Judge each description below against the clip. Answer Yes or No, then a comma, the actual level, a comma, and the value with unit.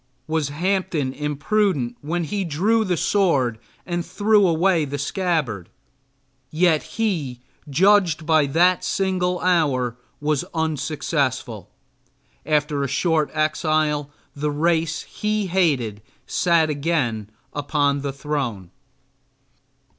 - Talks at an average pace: No, slow, 105 wpm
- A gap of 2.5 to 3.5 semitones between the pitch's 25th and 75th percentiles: No, average, 4.0 semitones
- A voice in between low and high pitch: Yes, medium, 155 Hz